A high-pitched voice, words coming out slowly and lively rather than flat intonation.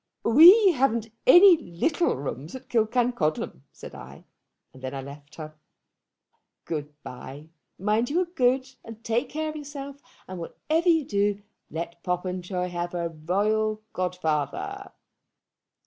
Yes: high, 205 Hz; slow, 130 wpm; wide, 8.2 semitones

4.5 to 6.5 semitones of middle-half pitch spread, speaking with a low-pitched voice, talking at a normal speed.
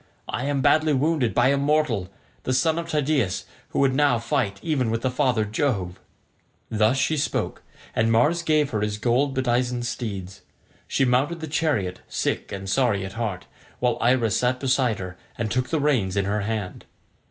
Yes: average, 5.0 semitones; low, 125 Hz; average, 175 wpm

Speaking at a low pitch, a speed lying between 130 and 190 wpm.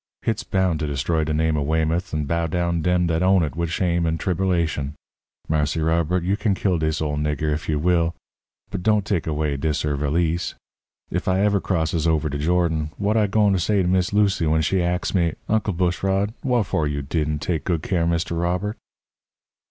No: very low, 85 Hz; fast, 205 wpm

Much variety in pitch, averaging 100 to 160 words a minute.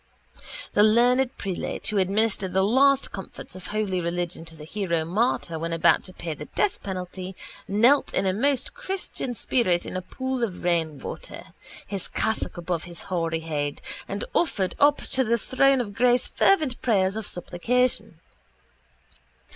Yes: wide, 6.0 semitones; average, 155 wpm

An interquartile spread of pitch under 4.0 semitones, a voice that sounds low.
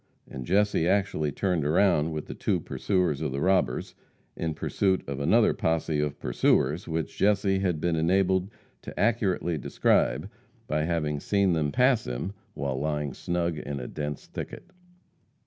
No: average, 4.3 semitones; very low, 80 Hz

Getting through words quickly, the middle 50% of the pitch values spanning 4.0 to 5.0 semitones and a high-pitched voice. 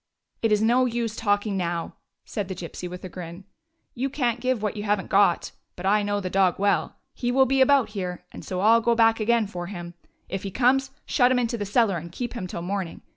Yes: fast, 255 wpm; average, 4.3 semitones; high, 205 Hz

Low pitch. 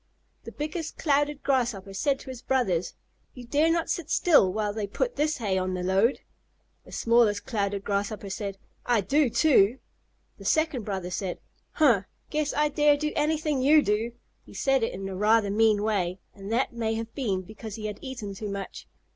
No: high, 225 Hz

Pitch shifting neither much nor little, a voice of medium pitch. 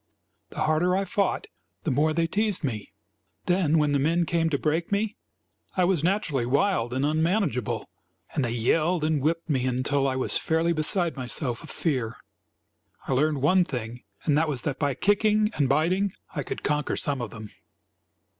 Yes: average, 4.6 semitones; medium, 155 Hz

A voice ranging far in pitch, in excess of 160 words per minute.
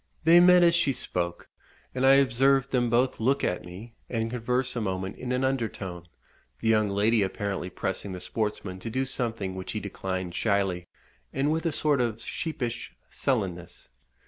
Yes: wide, 5.7 semitones; average, 175 wpm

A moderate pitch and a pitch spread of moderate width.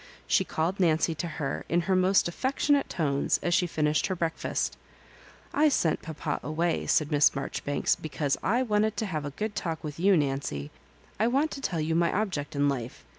Yes: medium, 165 Hz; average, 4.8 semitones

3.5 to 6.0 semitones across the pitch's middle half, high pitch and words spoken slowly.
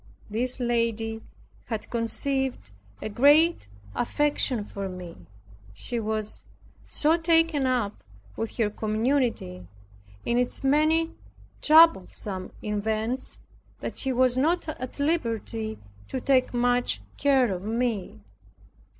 Yes: average, 4.3 semitones; high, 240 Hz; slow, 105 wpm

